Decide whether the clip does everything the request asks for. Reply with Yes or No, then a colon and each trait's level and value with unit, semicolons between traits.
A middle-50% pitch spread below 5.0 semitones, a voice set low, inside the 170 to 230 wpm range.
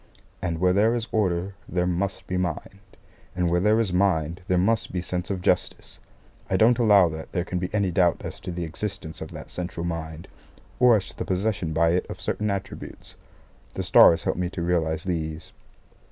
Yes: narrow, 2.6 semitones; very low, 90 Hz; average, 200 wpm